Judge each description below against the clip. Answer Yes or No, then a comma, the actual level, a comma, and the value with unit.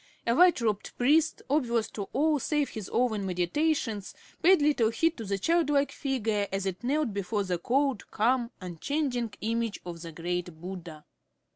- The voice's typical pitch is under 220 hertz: No, high, 230 Hz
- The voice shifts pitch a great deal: Yes, wide, 6.6 semitones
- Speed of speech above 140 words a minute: Yes, average, 160 wpm